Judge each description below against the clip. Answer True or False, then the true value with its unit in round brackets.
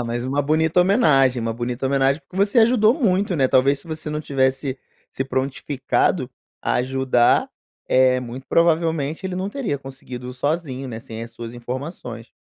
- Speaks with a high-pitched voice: False (135 Hz)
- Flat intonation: False (4.1 semitones)